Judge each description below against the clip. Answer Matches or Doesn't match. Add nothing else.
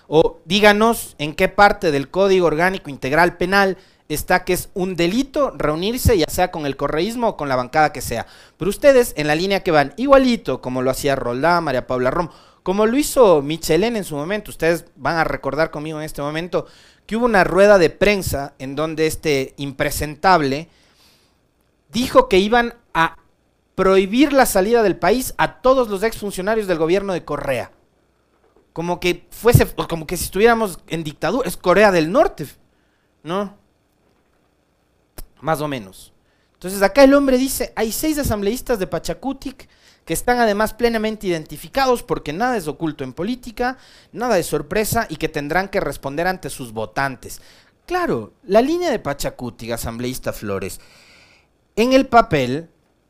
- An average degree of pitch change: Doesn't match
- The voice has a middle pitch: Matches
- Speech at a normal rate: Matches